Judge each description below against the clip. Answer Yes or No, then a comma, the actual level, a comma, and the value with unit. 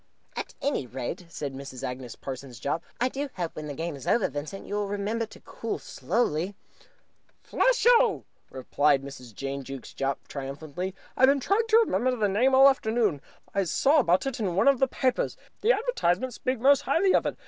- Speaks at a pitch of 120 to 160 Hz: No, high, 195 Hz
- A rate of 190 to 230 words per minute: Yes, average, 195 wpm